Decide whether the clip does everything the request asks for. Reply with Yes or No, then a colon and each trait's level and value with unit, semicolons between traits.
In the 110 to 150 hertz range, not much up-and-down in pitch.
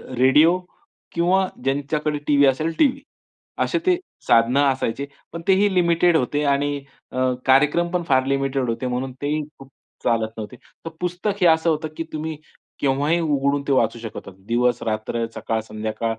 No: medium, 140 Hz; average, 4.7 semitones